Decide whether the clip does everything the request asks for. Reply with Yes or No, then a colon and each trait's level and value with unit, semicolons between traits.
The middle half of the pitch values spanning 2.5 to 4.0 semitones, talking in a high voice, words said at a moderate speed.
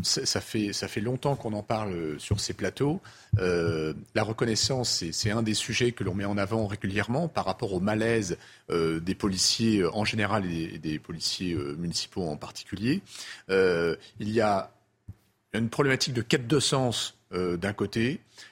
No: average, 3.7 semitones; low, 105 Hz; average, 170 wpm